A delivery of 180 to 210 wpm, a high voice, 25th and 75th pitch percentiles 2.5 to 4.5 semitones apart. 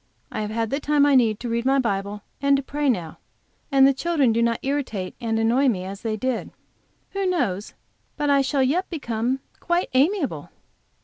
Yes: average, 195 wpm; very high, 255 Hz; average, 4.2 semitones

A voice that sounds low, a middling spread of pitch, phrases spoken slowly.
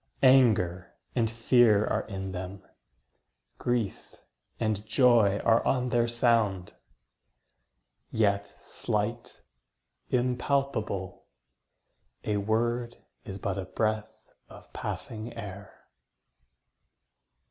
Yes: low, 110 Hz; average, 3.1 semitones; slow, 85 wpm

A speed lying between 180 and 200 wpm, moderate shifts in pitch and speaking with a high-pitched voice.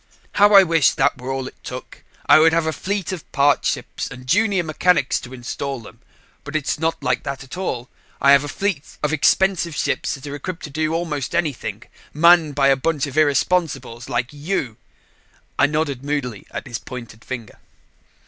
No: average, 190 wpm; average, 3.9 semitones; medium, 145 Hz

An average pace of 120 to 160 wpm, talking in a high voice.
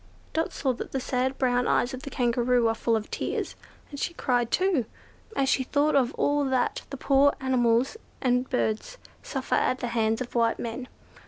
No: average, 190 wpm; very high, 255 Hz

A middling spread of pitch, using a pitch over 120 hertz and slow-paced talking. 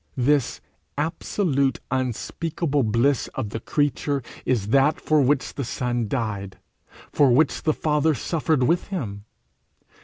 Yes: average, 3.9 semitones; low, 135 Hz; slow, 125 wpm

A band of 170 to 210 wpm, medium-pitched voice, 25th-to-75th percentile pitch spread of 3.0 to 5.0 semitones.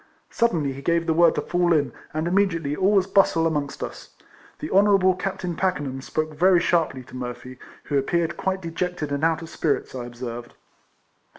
Yes: average, 180 wpm; medium, 165 Hz; average, 4.2 semitones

